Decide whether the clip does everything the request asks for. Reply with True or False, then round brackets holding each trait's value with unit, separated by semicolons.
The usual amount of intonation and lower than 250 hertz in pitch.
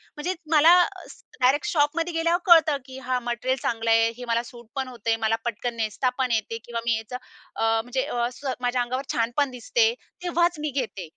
False (4.2 semitones; 255 Hz)